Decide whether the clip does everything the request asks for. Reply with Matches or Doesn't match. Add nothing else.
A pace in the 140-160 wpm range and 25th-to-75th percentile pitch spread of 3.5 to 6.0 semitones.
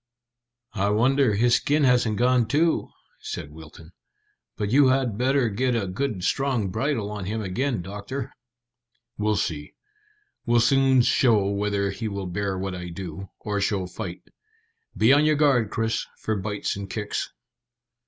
Matches